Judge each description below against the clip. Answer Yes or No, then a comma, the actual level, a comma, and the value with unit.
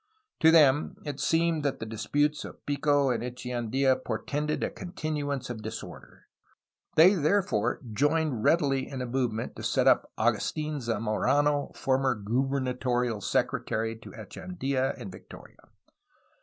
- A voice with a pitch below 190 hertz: Yes, low, 135 Hz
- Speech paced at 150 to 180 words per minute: No, average, 140 wpm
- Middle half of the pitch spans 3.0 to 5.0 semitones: Yes, average, 3.6 semitones